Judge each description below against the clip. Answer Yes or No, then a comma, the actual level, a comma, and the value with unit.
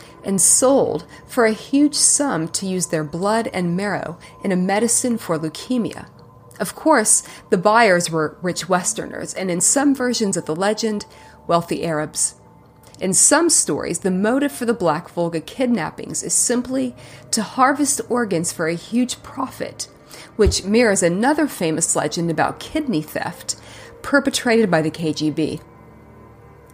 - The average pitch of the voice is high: Yes, high, 195 Hz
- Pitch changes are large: Yes, wide, 6.4 semitones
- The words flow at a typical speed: Yes, average, 145 wpm